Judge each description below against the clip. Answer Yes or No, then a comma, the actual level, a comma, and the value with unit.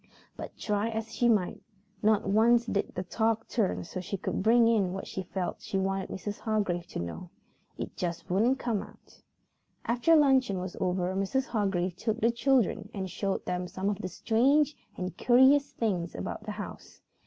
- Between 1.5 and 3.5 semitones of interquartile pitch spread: No, average, 4.0 semitones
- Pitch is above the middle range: Yes, high, 205 Hz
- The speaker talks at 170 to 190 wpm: Yes, average, 180 wpm